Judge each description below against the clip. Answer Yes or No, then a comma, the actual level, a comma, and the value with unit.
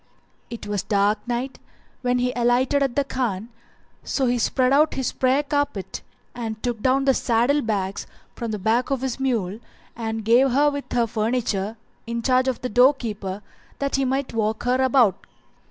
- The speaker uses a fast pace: No, average, 180 wpm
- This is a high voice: Yes, high, 245 Hz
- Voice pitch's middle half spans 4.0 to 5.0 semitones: No, average, 3.2 semitones